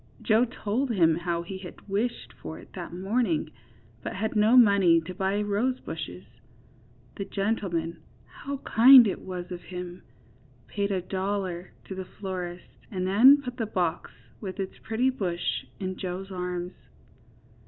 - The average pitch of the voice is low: No, high, 190 Hz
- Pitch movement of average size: Yes, average, 3.4 semitones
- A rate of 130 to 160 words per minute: Yes, average, 150 wpm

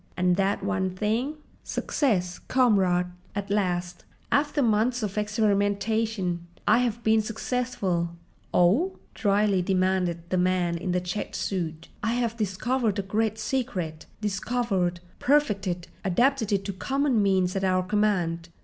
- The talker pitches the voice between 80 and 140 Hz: No, high, 200 Hz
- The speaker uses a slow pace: Yes, slow, 120 wpm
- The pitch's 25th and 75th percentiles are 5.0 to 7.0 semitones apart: No, average, 3.7 semitones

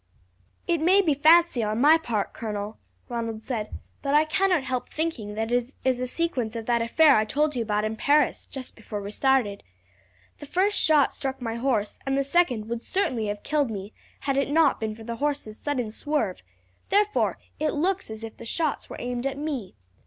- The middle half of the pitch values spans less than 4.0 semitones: No, wide, 5.4 semitones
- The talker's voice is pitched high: Yes, very high, 255 Hz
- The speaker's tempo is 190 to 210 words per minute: Yes, average, 200 wpm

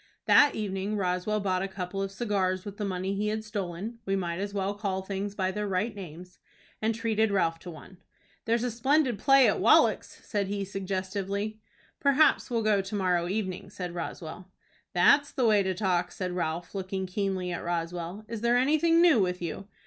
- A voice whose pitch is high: Yes, high, 195 Hz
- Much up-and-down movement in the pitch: No, average, 2.8 semitones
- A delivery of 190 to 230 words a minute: Yes, average, 195 wpm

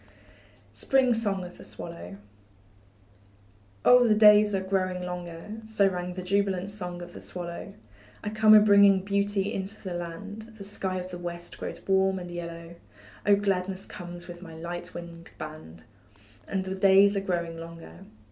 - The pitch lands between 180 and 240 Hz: Yes, medium, 185 Hz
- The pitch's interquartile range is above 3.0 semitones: No, narrow, 2.6 semitones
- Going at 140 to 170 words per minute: Yes, average, 165 wpm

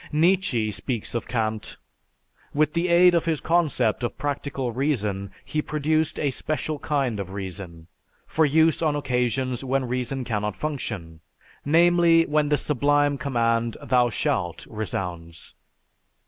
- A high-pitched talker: No, low, 135 Hz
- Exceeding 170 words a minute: No, slow, 135 wpm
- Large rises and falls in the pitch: Yes, wide, 5.7 semitones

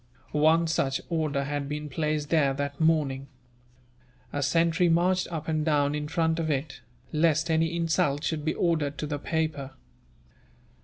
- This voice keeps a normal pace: Yes, average, 155 wpm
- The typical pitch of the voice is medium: Yes, medium, 155 Hz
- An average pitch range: No, narrow, 2.1 semitones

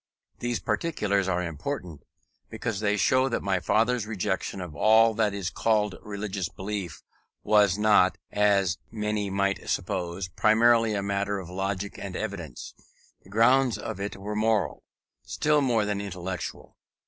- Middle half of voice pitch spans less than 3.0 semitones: Yes, narrow, 2.4 semitones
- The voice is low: Yes, low, 100 Hz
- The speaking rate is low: No, average, 145 wpm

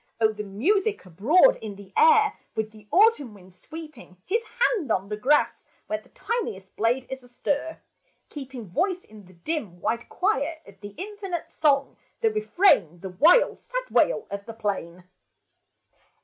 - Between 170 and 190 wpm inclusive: No, average, 160 wpm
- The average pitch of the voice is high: Yes, very high, 260 Hz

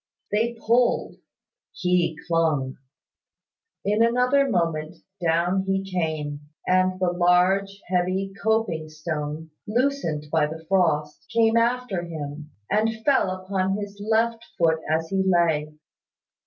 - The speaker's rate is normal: No, slow, 115 wpm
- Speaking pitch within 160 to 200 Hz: Yes, medium, 185 Hz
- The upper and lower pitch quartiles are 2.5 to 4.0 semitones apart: No, average, 4.8 semitones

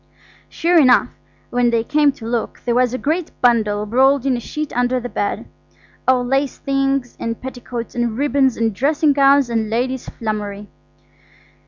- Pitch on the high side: Yes, very high, 250 Hz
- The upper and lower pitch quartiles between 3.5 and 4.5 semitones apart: No, average, 3.0 semitones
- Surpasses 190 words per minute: No, average, 160 wpm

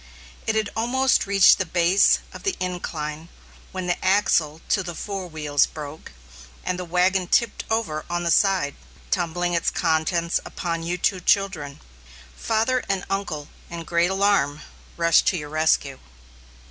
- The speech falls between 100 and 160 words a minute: Yes, average, 150 wpm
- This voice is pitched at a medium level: Yes, medium, 175 Hz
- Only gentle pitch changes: No, average, 3.6 semitones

